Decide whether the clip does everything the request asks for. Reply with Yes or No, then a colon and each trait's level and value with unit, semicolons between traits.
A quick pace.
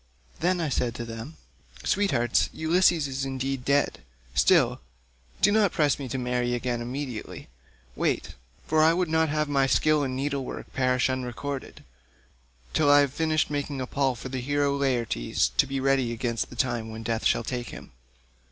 No: average, 165 wpm